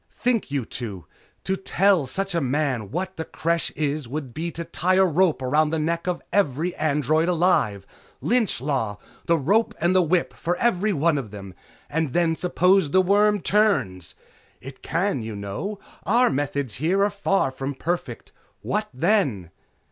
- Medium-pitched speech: Yes, medium, 165 Hz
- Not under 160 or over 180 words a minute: Yes, average, 170 wpm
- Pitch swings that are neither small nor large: No, wide, 5.7 semitones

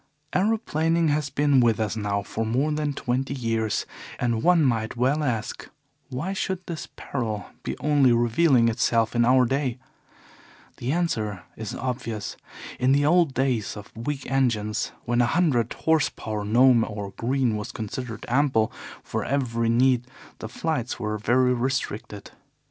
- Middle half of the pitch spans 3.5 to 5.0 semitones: Yes, average, 4.1 semitones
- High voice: No, low, 125 Hz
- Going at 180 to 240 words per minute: No, average, 150 wpm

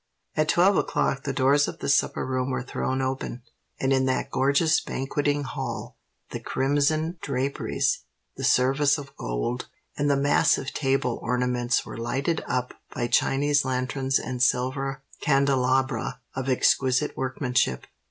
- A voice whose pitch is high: No, low, 135 Hz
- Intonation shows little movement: Yes, narrow, 1.9 semitones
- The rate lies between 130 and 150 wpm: Yes, average, 140 wpm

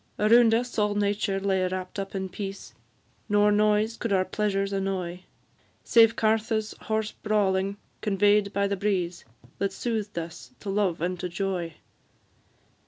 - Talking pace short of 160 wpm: Yes, average, 145 wpm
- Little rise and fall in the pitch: Yes, narrow, 1.9 semitones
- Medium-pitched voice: No, high, 200 Hz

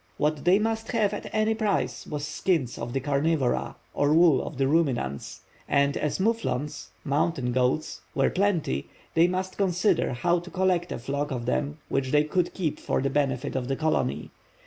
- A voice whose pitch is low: No, medium, 150 Hz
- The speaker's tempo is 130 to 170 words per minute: No, average, 180 wpm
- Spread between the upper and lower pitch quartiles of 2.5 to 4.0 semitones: No, average, 5.0 semitones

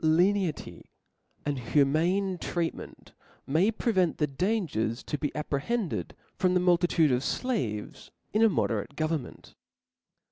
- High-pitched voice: No, medium, 165 Hz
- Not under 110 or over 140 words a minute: Yes, slow, 135 wpm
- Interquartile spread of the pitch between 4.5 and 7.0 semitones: Yes, average, 4.9 semitones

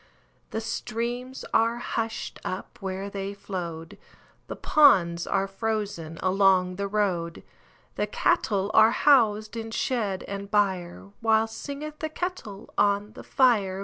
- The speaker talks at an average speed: No, slow, 115 wpm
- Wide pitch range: No, average, 3.0 semitones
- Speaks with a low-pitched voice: No, high, 205 Hz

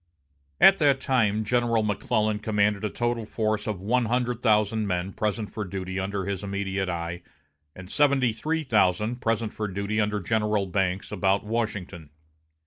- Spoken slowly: No, average, 155 wpm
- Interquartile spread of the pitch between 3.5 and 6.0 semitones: No, average, 2.8 semitones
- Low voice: Yes, low, 105 Hz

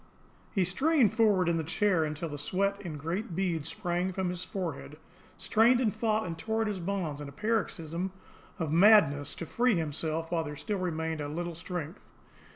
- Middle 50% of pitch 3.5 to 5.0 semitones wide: Yes, average, 4.3 semitones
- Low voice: No, medium, 175 Hz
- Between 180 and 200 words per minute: Yes, average, 185 wpm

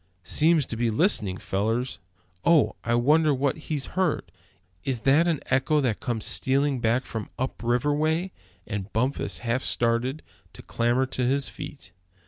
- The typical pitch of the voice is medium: No, low, 130 Hz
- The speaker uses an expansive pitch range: No, average, 4.0 semitones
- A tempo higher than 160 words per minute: No, average, 155 wpm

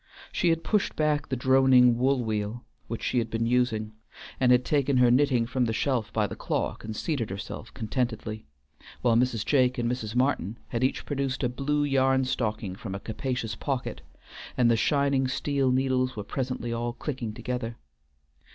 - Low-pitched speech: Yes, low, 125 Hz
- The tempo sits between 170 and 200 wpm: Yes, average, 180 wpm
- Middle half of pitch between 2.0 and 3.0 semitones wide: Yes, average, 2.7 semitones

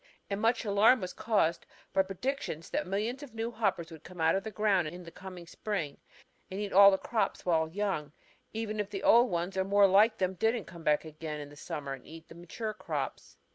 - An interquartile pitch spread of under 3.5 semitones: No, average, 4.3 semitones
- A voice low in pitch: No, high, 190 Hz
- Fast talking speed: Yes, fast, 215 wpm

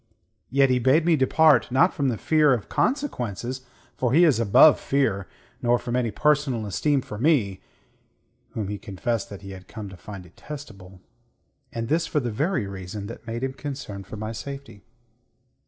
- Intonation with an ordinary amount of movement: No, wide, 5.8 semitones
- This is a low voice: Yes, low, 120 Hz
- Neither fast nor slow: Yes, average, 175 wpm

